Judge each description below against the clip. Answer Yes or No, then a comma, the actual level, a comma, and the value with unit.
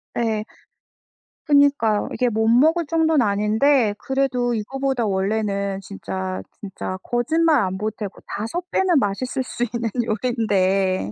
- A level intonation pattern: No, average, 5.1 semitones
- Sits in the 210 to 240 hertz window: Yes, high, 225 Hz